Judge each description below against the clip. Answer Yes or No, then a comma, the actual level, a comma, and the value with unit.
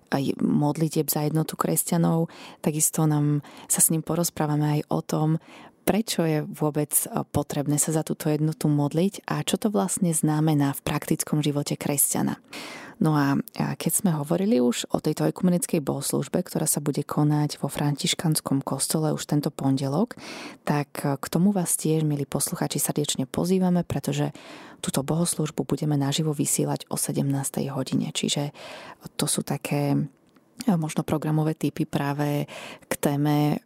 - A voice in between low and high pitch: Yes, medium, 155 Hz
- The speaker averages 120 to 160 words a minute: Yes, average, 145 wpm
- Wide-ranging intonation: No, average, 2.7 semitones